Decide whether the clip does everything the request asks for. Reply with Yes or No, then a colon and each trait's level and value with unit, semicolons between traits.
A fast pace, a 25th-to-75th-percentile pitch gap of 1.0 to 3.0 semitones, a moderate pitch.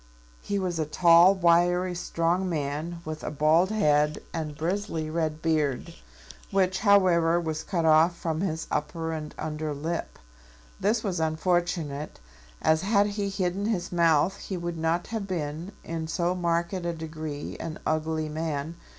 No: average, 150 wpm; narrow, 2.5 semitones; medium, 165 Hz